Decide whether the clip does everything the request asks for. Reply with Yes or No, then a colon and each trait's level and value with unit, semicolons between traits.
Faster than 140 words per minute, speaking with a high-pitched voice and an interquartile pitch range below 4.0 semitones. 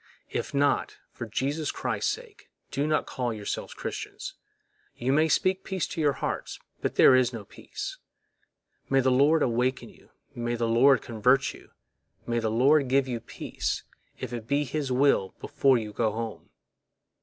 No: average, 165 wpm; low, 130 Hz; average, 3.4 semitones